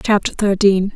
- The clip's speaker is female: Yes, female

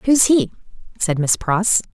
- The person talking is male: No, female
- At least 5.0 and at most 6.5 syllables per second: No, 4.0 syllables/s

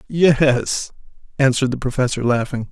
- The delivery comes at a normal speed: No, slow, 110 wpm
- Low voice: Yes, low, 130 Hz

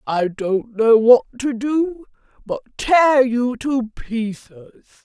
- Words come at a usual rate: No, slow, 130 wpm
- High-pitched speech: Yes, high, 240 Hz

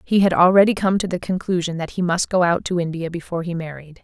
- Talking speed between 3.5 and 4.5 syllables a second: No, 6.4 syllables/s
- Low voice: No, medium, 175 Hz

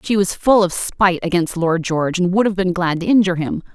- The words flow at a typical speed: No, fast, 255 wpm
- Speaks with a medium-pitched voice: Yes, medium, 180 Hz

